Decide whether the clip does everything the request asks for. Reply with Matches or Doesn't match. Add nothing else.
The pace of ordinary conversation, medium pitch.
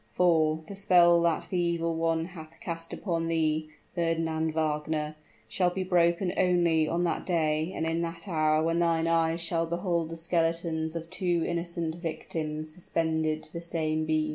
Matches